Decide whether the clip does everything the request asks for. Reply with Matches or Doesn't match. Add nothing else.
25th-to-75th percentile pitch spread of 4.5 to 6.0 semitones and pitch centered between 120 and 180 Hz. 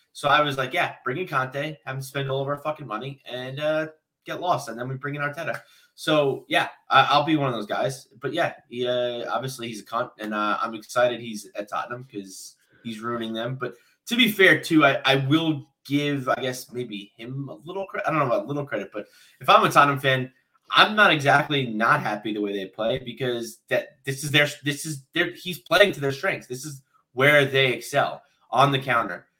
Doesn't match